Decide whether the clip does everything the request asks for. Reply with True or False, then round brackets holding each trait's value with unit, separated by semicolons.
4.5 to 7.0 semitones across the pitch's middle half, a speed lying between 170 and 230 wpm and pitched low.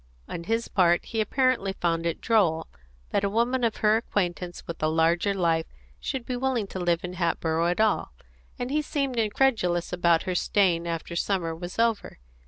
False (5.1 semitones; 185 wpm; 185 Hz)